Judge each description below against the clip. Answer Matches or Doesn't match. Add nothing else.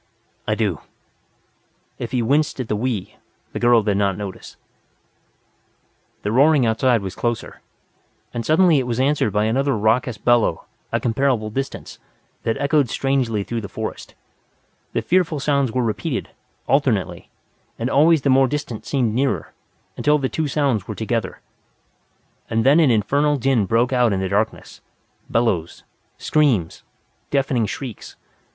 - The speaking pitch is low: Matches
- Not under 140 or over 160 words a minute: Matches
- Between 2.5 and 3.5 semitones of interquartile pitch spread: Doesn't match